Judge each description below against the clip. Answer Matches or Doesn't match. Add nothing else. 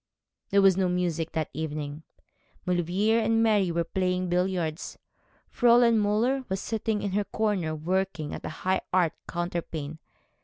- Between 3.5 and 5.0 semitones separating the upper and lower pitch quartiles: Matches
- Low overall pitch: Doesn't match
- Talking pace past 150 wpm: Doesn't match